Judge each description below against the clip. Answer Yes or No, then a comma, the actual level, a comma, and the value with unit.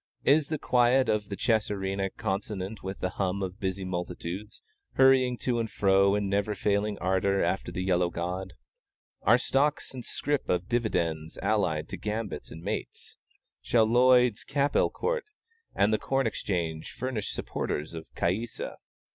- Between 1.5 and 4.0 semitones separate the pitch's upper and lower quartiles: No, average, 4.5 semitones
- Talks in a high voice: No, low, 100 Hz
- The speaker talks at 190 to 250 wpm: No, average, 155 wpm